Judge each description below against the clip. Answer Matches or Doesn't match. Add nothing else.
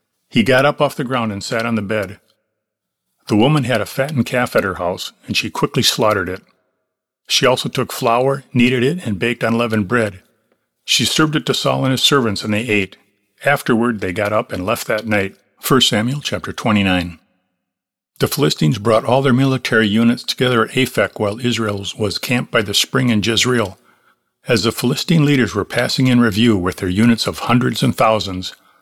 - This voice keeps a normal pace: Matches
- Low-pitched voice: Matches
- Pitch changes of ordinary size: Matches